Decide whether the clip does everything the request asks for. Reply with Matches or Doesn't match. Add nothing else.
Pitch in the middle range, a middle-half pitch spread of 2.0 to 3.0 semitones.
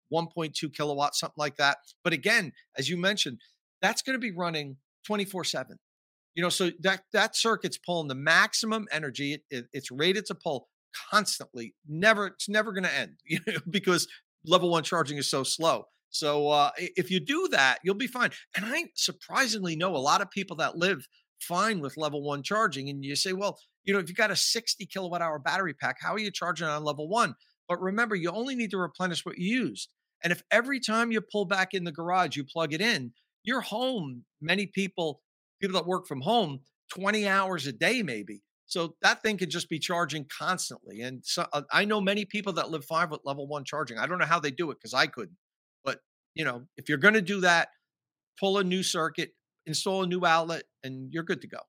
Doesn't match